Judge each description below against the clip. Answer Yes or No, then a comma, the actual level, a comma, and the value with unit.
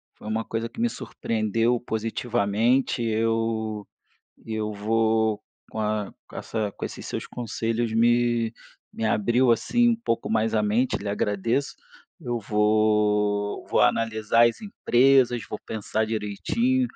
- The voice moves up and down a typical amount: No, narrow, 1.8 semitones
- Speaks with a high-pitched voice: No, low, 110 Hz